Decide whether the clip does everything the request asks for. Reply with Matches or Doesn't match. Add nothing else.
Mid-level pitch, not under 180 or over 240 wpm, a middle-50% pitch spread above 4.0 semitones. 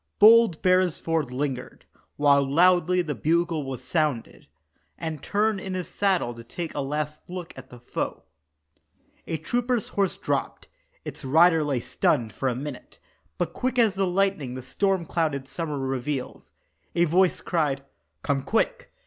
Doesn't match